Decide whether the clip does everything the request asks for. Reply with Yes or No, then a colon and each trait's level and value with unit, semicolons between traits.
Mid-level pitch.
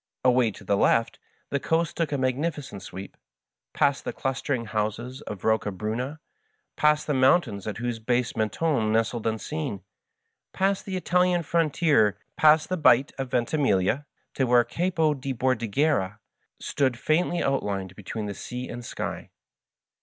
No: low, 125 Hz